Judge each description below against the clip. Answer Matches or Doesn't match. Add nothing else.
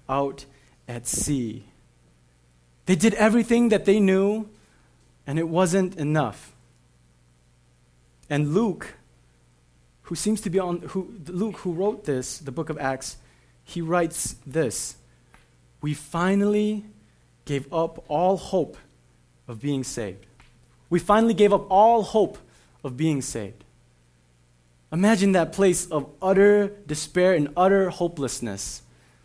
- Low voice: Doesn't match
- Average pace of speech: Doesn't match